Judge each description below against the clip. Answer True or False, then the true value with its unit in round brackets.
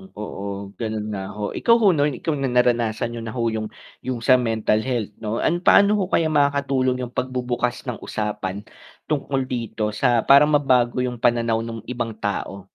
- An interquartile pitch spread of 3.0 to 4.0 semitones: True (3.4 semitones)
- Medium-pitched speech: False (120 Hz)